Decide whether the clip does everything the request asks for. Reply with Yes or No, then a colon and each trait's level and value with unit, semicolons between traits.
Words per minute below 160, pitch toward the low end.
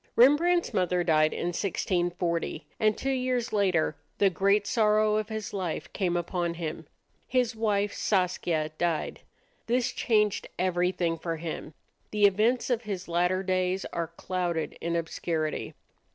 No: average, 140 wpm; medium, 185 Hz